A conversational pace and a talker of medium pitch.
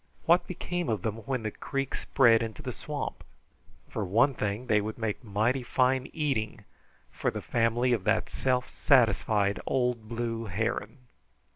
No: average, 155 wpm; low, 115 Hz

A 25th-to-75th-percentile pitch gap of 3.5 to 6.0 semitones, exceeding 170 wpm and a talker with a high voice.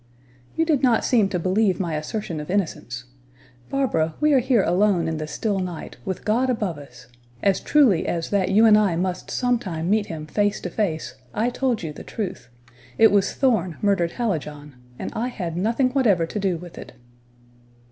Yes: average, 5.3 semitones; average, 190 wpm; high, 195 Hz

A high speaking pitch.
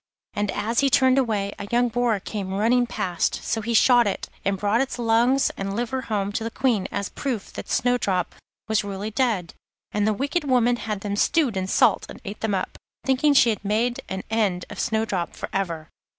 Yes: high, 220 Hz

